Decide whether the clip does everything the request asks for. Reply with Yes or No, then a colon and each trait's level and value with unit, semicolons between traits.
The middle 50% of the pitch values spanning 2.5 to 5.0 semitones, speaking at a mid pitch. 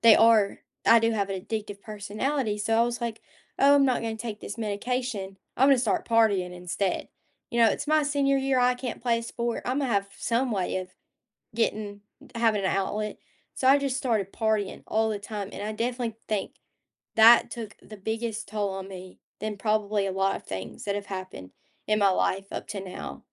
No: average, 3.1 semitones; high, 215 Hz